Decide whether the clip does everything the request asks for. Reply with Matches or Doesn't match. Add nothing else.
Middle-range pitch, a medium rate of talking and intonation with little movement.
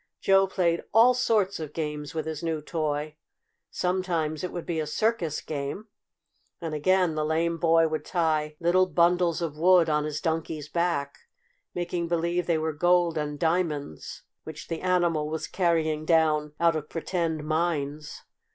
Matches